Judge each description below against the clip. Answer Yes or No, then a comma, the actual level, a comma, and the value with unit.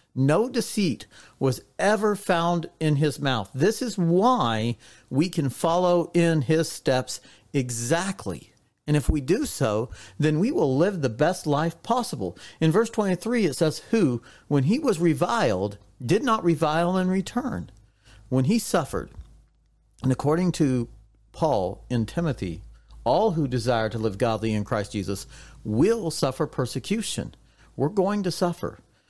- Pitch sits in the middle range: Yes, medium, 155 Hz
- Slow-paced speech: No, average, 145 wpm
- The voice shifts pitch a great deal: Yes, wide, 6.8 semitones